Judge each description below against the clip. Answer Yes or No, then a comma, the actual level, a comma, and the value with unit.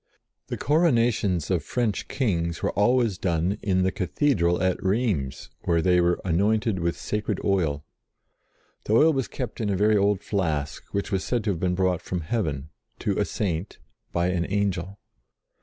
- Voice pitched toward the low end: Yes, very low, 95 Hz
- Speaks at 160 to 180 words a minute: Yes, average, 175 wpm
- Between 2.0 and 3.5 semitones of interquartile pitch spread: No, average, 3.9 semitones